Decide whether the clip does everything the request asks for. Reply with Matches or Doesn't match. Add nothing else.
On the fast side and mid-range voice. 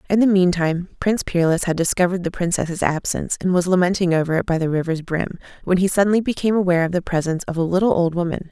Matches